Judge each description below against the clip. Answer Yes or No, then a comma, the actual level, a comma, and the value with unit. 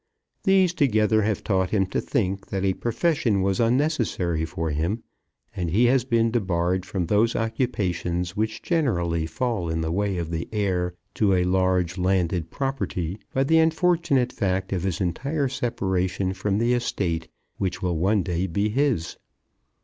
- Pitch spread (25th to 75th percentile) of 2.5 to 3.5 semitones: No, average, 4.9 semitones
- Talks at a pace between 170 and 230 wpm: No, average, 160 wpm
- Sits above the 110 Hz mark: No, very low, 95 Hz